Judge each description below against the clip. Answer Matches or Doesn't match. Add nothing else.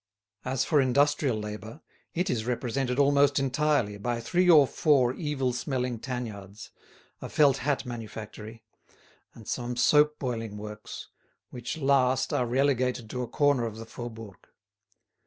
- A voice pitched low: Matches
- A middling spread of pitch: Matches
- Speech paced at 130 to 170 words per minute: Matches